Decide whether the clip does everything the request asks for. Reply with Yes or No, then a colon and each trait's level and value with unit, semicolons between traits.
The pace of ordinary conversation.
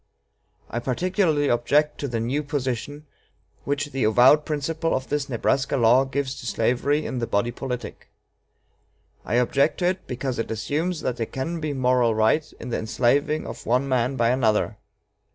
Yes: average, 170 wpm